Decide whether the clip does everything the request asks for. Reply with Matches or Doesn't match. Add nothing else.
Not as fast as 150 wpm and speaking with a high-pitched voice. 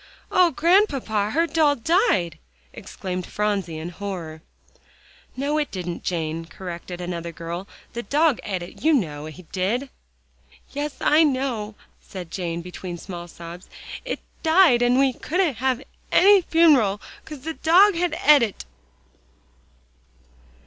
Matches